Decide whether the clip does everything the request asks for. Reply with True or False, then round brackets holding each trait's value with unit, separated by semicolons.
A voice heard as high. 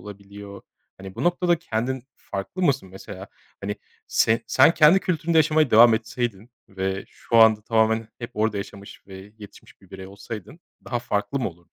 False (110 Hz)